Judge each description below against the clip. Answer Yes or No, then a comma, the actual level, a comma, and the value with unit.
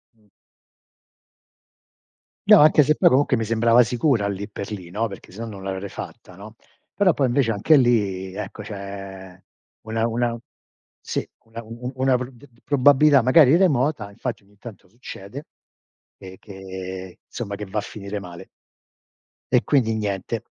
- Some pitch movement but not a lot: Yes, average, 4.3 semitones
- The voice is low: Yes, low, 110 Hz